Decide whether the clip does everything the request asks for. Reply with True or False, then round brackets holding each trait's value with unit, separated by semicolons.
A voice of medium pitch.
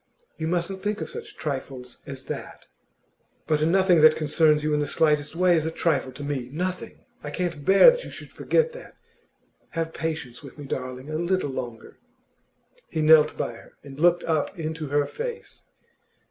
True (155 Hz)